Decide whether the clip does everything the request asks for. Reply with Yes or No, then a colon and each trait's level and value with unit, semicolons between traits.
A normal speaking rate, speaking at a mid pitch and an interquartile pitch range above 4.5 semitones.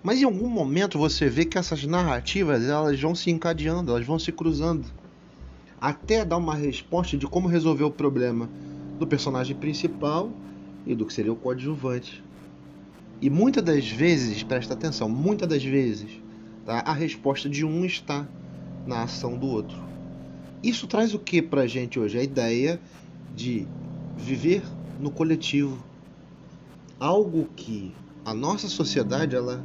Yes: average, 150 wpm; medium, 150 Hz; average, 5.2 semitones